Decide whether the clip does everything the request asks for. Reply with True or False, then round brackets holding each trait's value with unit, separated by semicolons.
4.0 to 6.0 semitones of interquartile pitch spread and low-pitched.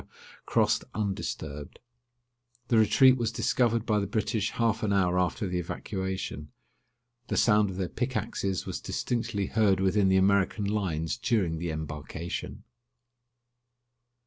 False (3.3 semitones; 100 Hz)